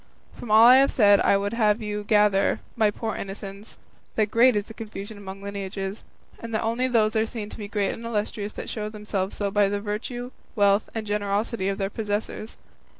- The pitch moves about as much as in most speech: No, narrow, 1.7 semitones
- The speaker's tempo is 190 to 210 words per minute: Yes, fast, 205 wpm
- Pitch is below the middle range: No, high, 210 Hz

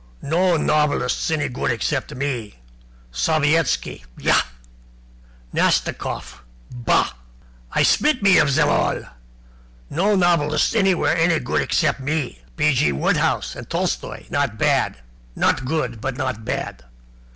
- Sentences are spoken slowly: Yes, slow, 120 wpm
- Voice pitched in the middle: Yes, medium, 150 Hz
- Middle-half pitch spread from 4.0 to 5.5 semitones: Yes, average, 4.4 semitones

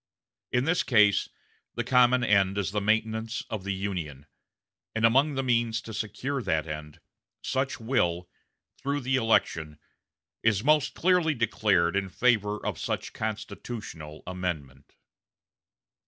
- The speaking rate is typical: No, slow, 130 wpm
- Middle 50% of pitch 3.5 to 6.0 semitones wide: Yes, average, 5.1 semitones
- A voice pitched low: Yes, low, 110 Hz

